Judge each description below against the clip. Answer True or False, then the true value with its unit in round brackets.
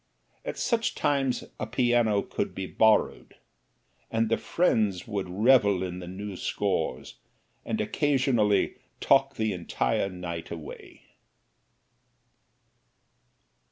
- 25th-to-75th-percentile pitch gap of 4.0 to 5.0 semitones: True (4.6 semitones)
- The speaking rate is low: True (105 wpm)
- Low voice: True (105 Hz)